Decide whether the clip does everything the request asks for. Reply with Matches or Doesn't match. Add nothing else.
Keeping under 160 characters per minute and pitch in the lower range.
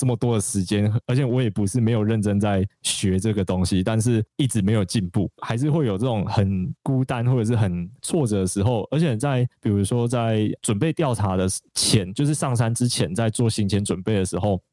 Doesn't match